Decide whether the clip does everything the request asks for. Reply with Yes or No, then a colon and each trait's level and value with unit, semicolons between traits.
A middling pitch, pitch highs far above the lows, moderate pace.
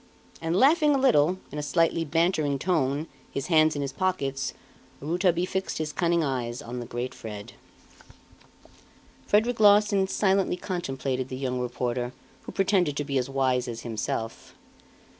Yes: medium, 150 Hz; wide, 6.1 semitones; average, 150 wpm